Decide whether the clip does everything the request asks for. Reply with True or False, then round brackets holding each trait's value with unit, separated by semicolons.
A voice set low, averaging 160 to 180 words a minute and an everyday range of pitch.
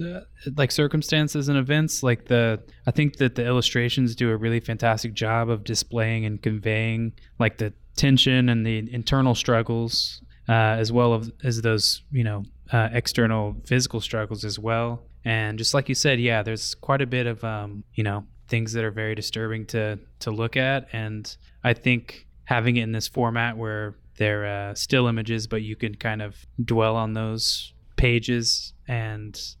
False (115 Hz; 175 wpm; 1.8 semitones)